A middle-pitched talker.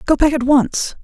No: very high, 275 Hz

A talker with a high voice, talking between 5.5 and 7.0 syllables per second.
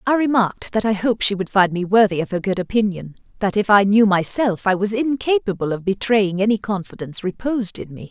Yes: high, 205 Hz; 5.9 syllables/s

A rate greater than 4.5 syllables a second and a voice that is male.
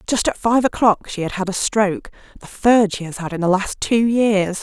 No: 5.1 syllables/s; female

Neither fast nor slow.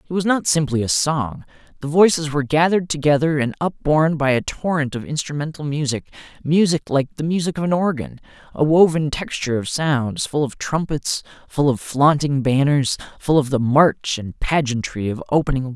Yes: average, 180 wpm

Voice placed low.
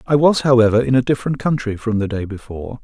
Yes: low, 120 Hz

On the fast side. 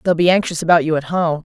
Yes: fast, 275 wpm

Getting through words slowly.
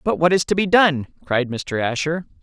No: fast, 225 wpm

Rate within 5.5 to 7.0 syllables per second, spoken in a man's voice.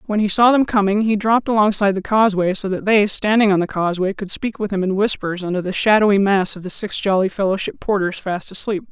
No: 6.2 syllables/s; female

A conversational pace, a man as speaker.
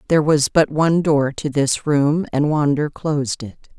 No: average, 190 wpm; female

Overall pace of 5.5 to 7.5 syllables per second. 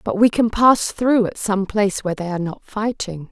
No: 5.3 syllables/s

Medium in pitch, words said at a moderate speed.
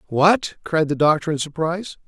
Yes: medium, 160 Hz; average, 175 wpm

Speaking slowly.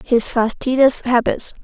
Yes: slow, 110 wpm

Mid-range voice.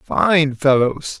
Yes: medium, 150 Hz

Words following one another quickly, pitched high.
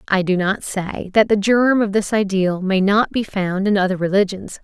Yes: fast, 220 wpm; high, 200 Hz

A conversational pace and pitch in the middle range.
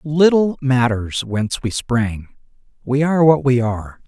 No: average, 145 wpm; low, 130 Hz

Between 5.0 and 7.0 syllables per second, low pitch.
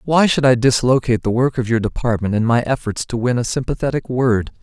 Yes: 5.9 syllables/s; low, 125 Hz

